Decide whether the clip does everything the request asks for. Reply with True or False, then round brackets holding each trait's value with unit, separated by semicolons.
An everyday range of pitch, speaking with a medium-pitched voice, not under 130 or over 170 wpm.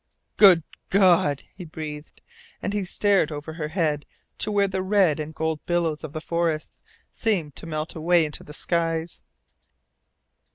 True (3.2 semitones; 165 Hz; 155 wpm)